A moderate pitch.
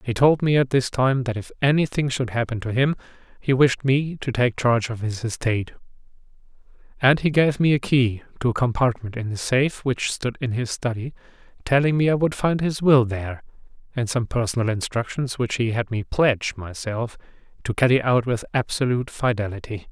No: low, 125 Hz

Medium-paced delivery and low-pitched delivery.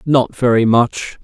Yes: average, 145 wpm; low, 120 Hz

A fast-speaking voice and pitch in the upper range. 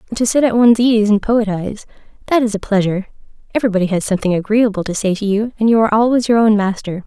Yes: fast, 210 wpm; high, 215 Hz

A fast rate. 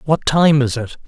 Yes: fast, 225 wpm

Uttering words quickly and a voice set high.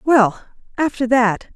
No: slow, 115 wpm; high, 245 Hz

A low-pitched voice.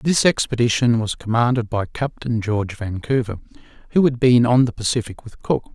Yes: low, 120 Hz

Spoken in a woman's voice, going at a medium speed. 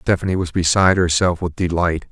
No: male; average, 170 wpm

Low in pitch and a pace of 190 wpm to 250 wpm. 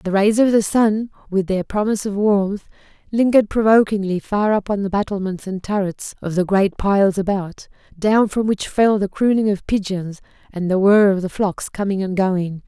No: high, 200 Hz; average, 195 wpm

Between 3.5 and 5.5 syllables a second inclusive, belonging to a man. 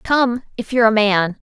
No: 5.0 syllables/s; female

